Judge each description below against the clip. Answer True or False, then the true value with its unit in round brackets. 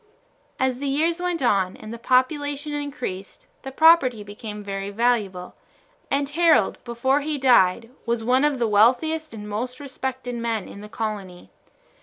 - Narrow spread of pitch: False (5.3 semitones)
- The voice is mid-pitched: False (245 Hz)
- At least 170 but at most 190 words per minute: False (150 wpm)